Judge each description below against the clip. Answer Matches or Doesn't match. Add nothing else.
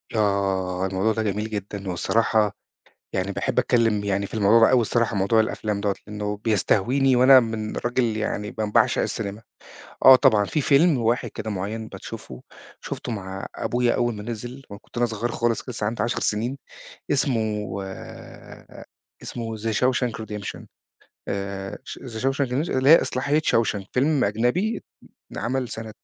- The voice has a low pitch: Matches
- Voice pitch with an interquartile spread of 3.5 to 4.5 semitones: Doesn't match